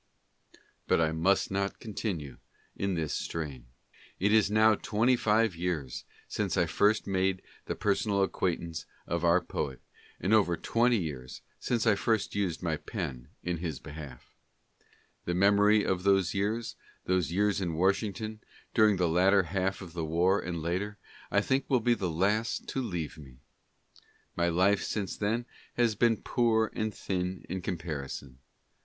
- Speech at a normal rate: Yes, average, 160 wpm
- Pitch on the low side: Yes, very low, 95 Hz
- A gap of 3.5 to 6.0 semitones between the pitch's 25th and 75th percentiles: Yes, average, 3.9 semitones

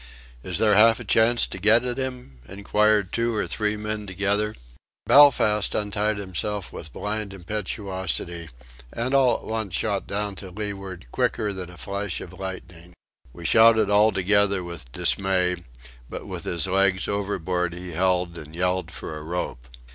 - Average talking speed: Yes, average, 160 wpm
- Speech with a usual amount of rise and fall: Yes, average, 3.0 semitones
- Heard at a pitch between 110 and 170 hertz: No, low, 100 Hz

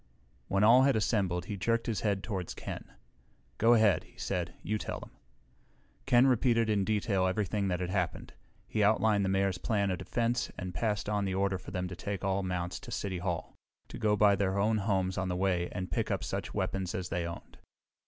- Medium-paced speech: No, fast, 210 wpm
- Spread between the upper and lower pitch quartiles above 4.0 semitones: No, average, 2.7 semitones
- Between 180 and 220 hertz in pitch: No, low, 100 Hz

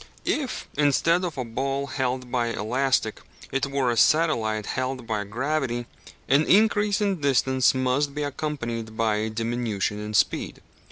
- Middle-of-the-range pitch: No, low, 130 Hz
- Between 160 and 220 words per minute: No, average, 150 wpm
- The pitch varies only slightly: No, average, 4.0 semitones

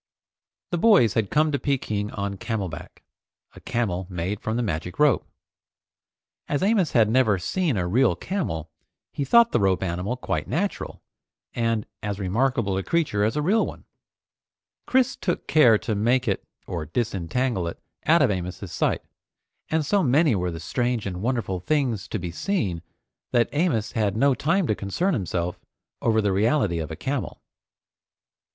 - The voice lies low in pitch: Yes, low, 110 Hz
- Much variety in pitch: Yes, wide, 7.1 semitones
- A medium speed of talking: Yes, average, 165 wpm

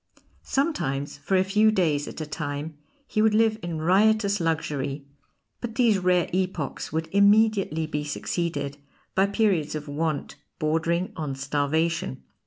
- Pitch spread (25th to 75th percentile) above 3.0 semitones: Yes, average, 5.3 semitones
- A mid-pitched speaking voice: Yes, medium, 165 Hz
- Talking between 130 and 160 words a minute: Yes, average, 140 wpm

